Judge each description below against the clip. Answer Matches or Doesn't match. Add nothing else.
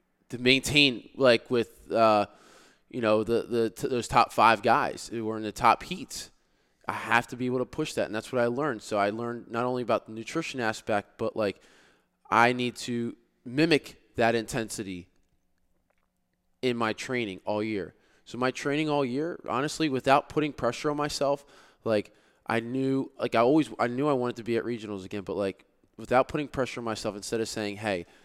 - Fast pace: Doesn't match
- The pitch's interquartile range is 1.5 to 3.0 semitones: Doesn't match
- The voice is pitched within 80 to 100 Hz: Doesn't match